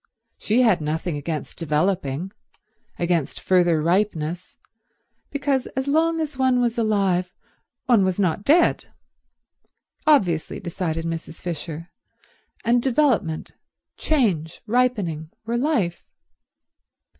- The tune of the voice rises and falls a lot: Yes, wide, 7.0 semitones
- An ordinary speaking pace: No, slow, 100 wpm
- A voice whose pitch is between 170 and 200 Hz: Yes, high, 190 Hz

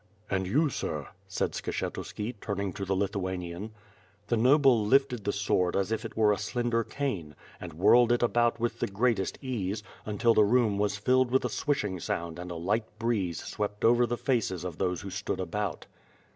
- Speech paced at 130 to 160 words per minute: No, average, 185 wpm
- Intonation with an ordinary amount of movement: Yes, average, 4.1 semitones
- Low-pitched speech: Yes, low, 105 Hz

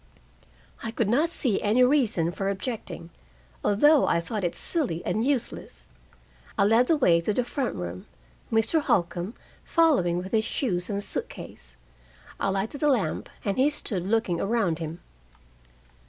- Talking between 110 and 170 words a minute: Yes, average, 155 wpm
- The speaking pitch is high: Yes, high, 210 Hz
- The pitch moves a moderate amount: No, wide, 6.2 semitones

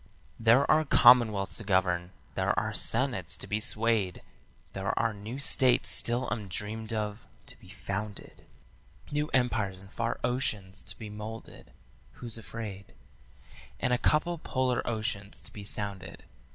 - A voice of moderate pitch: No, low, 110 Hz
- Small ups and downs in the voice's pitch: No, average, 3.4 semitones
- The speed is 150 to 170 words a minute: No, average, 140 wpm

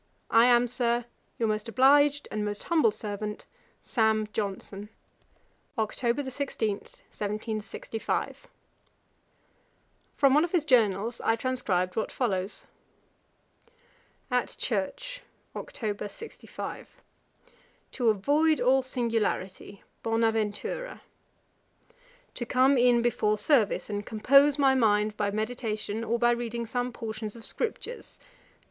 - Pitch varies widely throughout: No, average, 3.6 semitones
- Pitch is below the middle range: No, high, 230 Hz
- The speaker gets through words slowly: Yes, slow, 105 wpm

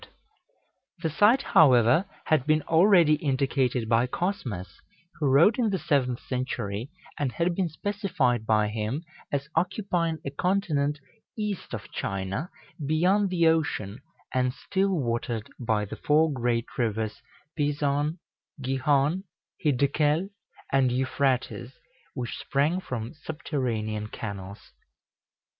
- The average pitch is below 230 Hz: Yes, medium, 140 Hz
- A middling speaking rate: No, slow, 115 wpm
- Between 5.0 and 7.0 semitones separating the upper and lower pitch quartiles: Yes, wide, 5.5 semitones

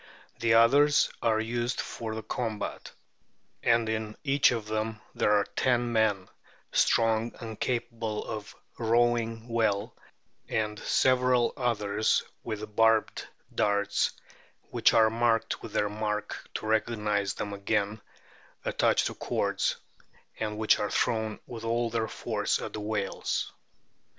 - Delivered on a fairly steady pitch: Yes, narrow, 1.7 semitones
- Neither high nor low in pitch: No, low, 110 Hz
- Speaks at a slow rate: Yes, slow, 125 wpm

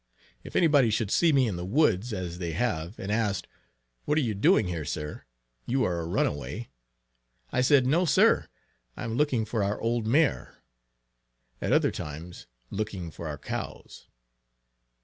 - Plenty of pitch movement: Yes, wide, 6.5 semitones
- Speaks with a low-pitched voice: Yes, low, 105 Hz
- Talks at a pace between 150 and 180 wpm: Yes, average, 170 wpm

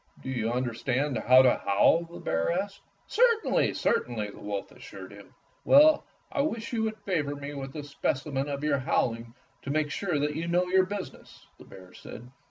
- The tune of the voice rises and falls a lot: Yes, wide, 6.7 semitones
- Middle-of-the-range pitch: Yes, medium, 145 Hz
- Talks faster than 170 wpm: Yes, average, 185 wpm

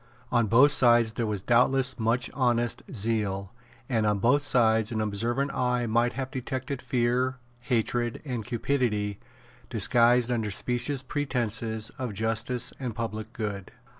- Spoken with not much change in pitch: Yes, narrow, 2.3 semitones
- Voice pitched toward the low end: Yes, low, 120 Hz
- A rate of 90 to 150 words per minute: Yes, slow, 135 wpm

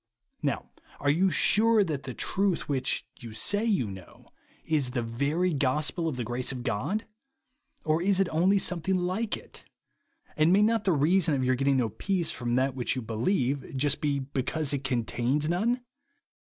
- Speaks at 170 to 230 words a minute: Yes, average, 180 wpm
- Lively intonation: Yes, wide, 6.2 semitones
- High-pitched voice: No, medium, 145 Hz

